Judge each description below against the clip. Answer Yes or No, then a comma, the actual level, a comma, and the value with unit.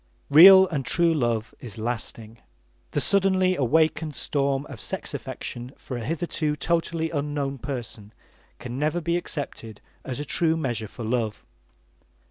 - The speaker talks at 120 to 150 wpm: Yes, average, 140 wpm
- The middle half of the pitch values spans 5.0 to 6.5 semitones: Yes, wide, 5.4 semitones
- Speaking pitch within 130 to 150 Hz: Yes, medium, 140 Hz